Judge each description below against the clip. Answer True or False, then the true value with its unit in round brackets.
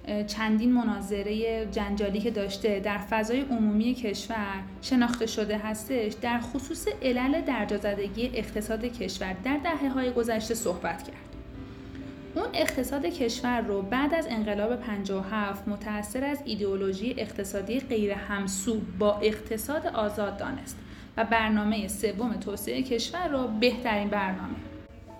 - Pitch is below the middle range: False (220 Hz)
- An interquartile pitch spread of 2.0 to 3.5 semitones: True (3.0 semitones)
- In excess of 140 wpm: False (120 wpm)